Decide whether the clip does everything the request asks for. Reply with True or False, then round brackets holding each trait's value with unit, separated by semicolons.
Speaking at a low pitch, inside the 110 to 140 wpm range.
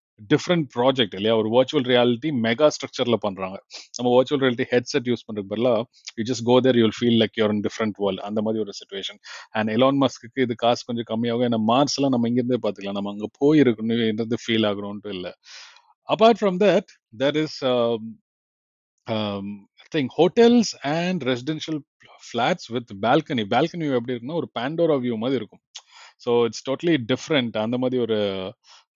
True (120 Hz; 120 wpm)